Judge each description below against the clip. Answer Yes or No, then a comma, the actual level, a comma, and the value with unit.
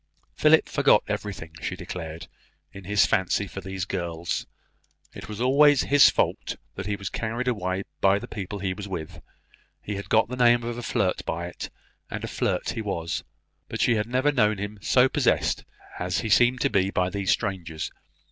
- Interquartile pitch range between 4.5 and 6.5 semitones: No, average, 4.1 semitones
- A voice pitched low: Yes, low, 100 Hz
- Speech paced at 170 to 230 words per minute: Yes, average, 190 wpm